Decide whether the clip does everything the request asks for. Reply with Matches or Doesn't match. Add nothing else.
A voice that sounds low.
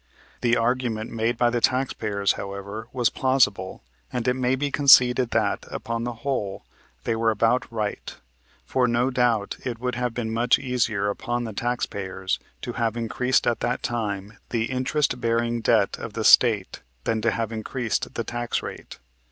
Matches